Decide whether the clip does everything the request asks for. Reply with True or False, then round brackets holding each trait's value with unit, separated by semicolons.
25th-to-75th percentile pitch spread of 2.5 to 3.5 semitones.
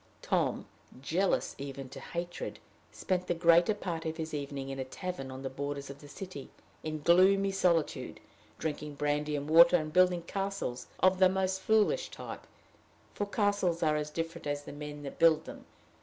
False (4.1 semitones)